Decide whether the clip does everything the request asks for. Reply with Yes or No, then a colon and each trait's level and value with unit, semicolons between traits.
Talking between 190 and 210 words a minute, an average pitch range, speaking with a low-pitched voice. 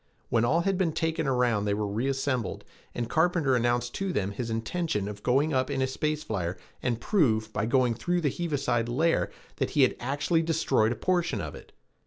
No: average, 200 wpm; wide, 5.7 semitones; low, 130 Hz